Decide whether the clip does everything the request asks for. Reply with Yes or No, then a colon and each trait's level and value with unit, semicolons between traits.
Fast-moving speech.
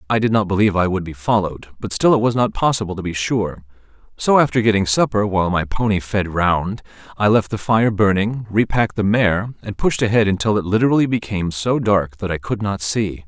Yes: fast, 215 wpm